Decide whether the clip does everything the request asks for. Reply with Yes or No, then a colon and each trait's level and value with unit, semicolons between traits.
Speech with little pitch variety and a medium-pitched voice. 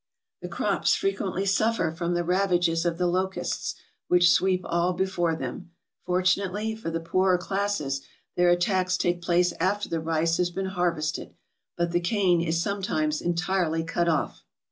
Yes: narrow, 2.0 semitones; medium, 175 Hz